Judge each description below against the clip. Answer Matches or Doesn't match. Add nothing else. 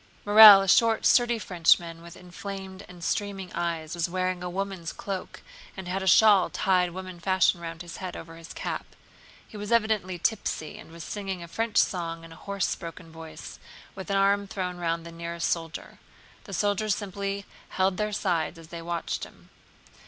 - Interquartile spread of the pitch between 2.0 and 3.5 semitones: Matches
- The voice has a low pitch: Doesn't match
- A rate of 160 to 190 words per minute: Matches